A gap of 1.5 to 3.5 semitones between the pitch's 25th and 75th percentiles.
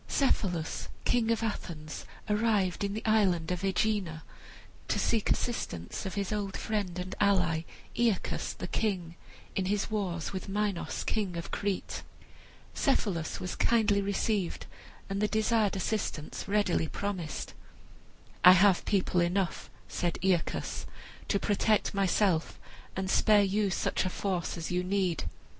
Yes: average, 2.8 semitones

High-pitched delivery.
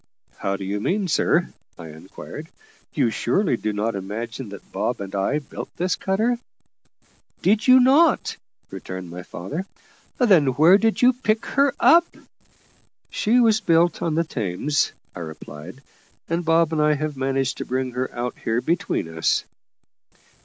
No: medium, 145 Hz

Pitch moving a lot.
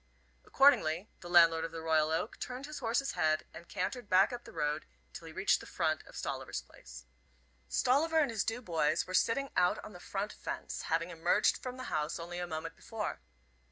Yes: wide, 6.5 semitones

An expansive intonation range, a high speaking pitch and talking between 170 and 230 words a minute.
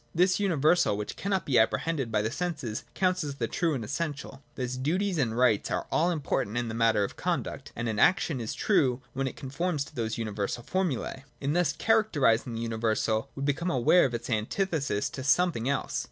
No: wide, 6.7 semitones; low, 135 Hz; average, 195 wpm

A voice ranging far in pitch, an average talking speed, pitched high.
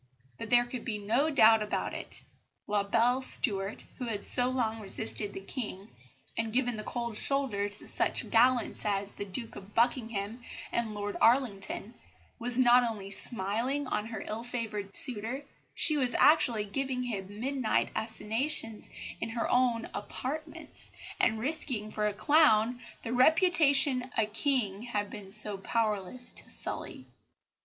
No: average, 3.5 semitones; average, 150 wpm; high, 230 Hz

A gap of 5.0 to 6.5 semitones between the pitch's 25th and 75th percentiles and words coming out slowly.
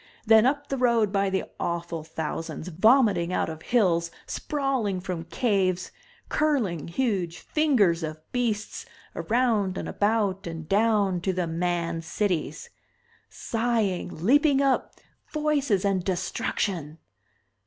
Yes: wide, 5.6 semitones; slow, 120 wpm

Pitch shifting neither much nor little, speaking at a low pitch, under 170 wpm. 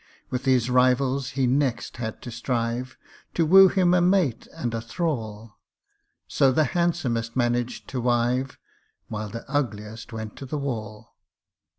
Yes: average, 3.3 semitones; low, 125 Hz; average, 150 wpm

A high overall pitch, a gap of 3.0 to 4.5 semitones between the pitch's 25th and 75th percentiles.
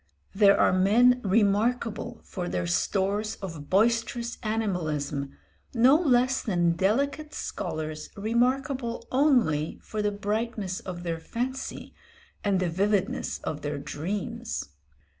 No: high, 210 Hz; average, 5.1 semitones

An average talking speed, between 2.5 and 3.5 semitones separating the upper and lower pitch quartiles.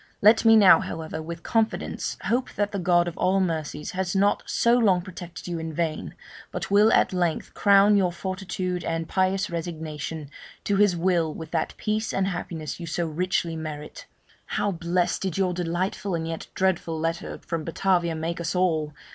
Yes: average, 180 wpm; average, 2.9 semitones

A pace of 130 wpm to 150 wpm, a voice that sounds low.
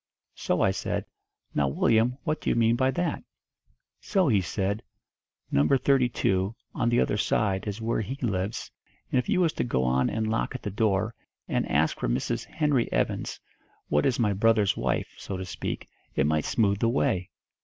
No: average, 185 wpm; low, 110 Hz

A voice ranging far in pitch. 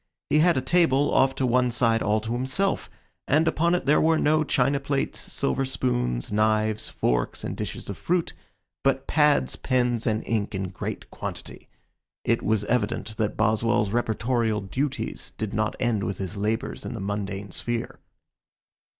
No: average, 4.5 semitones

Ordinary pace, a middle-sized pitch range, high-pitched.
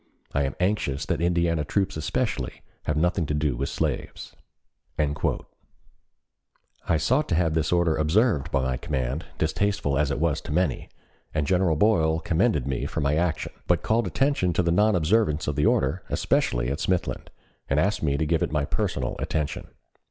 No: average, 175 wpm; average, 3.6 semitones; very low, 80 Hz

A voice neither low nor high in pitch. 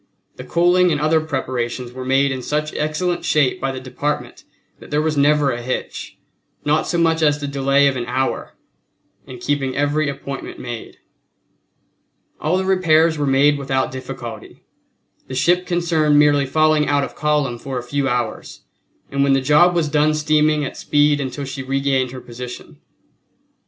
Yes: medium, 145 Hz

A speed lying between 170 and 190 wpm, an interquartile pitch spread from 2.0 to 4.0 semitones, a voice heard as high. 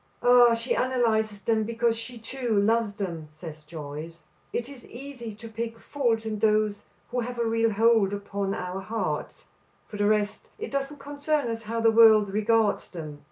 Yes: average, 175 wpm; narrow, 2.6 semitones; high, 225 Hz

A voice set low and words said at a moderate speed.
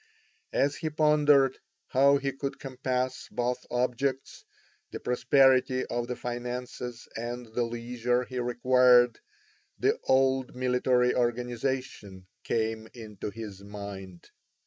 No: low, 125 Hz; slow, 110 wpm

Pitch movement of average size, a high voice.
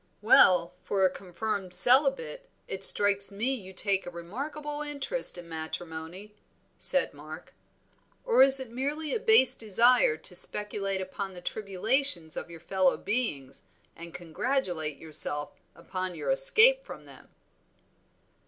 No: wide, 7.4 semitones; high, 200 Hz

